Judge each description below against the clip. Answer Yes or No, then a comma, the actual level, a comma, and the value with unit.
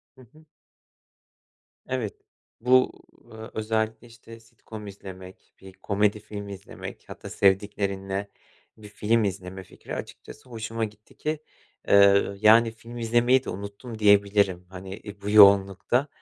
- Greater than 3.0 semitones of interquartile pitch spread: No, narrow, 2.5 semitones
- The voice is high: No, low, 105 Hz